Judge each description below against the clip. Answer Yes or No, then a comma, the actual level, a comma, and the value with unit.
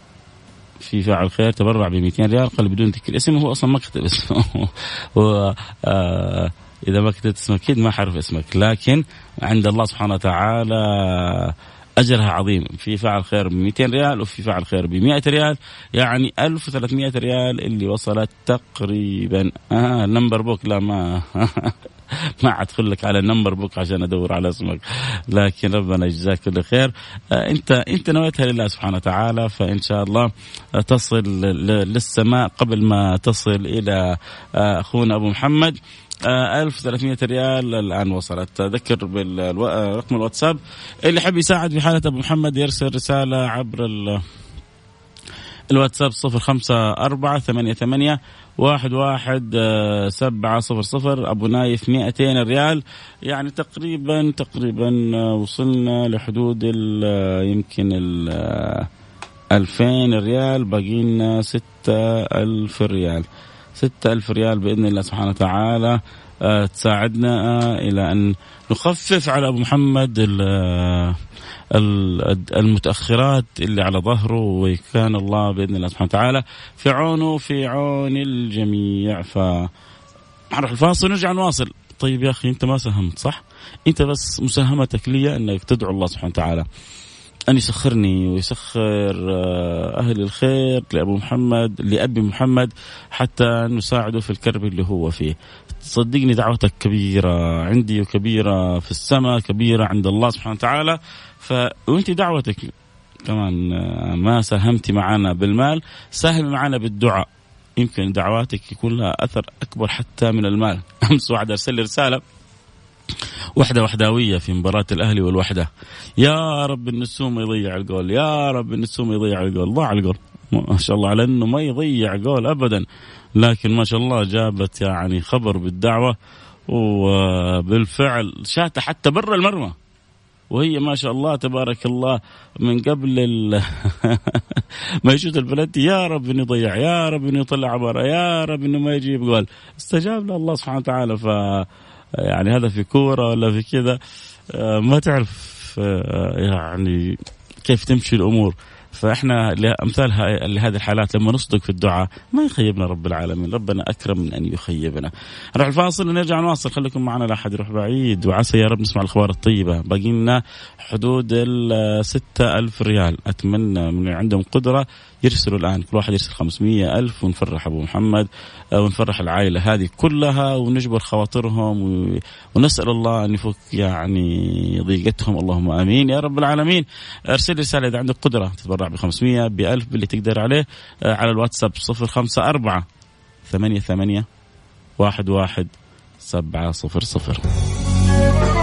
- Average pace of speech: No, slow, 130 wpm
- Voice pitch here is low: Yes, low, 110 Hz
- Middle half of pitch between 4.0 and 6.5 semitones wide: Yes, average, 4.5 semitones